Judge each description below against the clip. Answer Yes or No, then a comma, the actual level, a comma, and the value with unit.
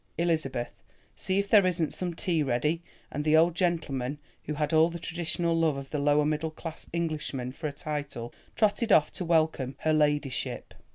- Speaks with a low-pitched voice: No, medium, 155 Hz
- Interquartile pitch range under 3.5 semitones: Yes, narrow, 2.6 semitones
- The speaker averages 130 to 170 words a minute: No, average, 180 wpm